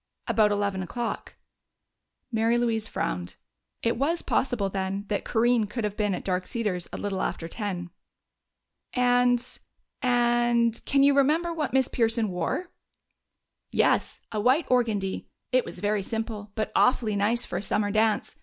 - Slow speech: No, average, 150 wpm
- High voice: Yes, high, 225 Hz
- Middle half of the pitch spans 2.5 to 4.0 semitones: Yes, average, 3.3 semitones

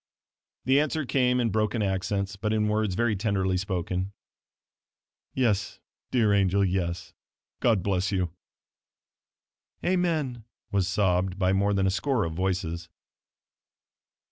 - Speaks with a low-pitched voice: Yes, low, 100 Hz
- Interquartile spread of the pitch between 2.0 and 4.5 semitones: Yes, average, 3.3 semitones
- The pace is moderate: No, slow, 120 wpm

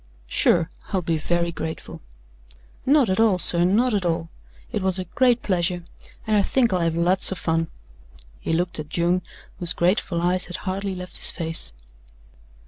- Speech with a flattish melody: Yes, narrow, 2.2 semitones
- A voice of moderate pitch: Yes, medium, 180 Hz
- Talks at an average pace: Yes, average, 175 wpm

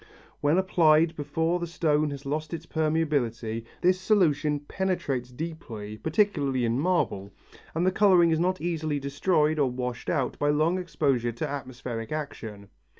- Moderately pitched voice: Yes, medium, 150 Hz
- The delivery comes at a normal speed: Yes, average, 150 wpm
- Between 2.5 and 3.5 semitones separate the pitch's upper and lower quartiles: No, average, 4.5 semitones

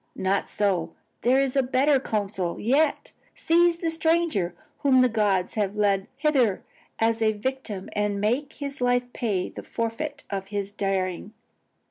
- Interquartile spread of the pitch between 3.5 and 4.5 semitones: No, wide, 5.4 semitones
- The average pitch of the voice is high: Yes, high, 225 Hz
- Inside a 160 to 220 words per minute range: No, average, 150 wpm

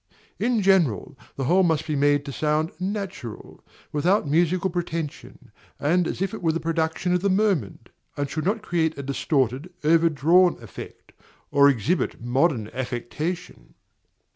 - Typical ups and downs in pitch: Yes, average, 4.2 semitones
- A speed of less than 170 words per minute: Yes, average, 145 wpm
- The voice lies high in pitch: No, medium, 160 Hz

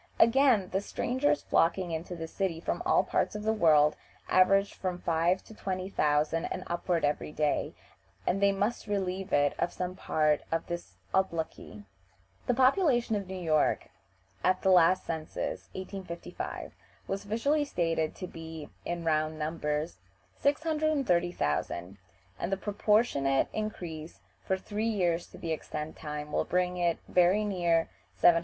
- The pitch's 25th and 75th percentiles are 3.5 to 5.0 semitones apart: Yes, average, 3.8 semitones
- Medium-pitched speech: Yes, medium, 180 Hz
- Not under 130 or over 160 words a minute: Yes, average, 150 wpm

